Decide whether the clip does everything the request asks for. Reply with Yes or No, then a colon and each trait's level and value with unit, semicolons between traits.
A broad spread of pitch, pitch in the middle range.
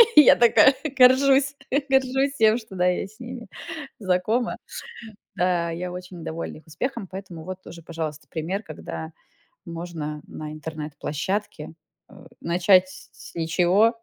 Yes: wide, 5.7 semitones; medium, 180 Hz